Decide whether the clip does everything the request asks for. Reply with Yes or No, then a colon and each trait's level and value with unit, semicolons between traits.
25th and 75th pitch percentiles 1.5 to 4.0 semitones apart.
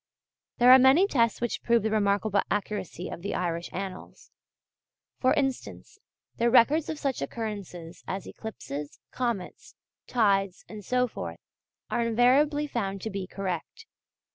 No: average, 4.4 semitones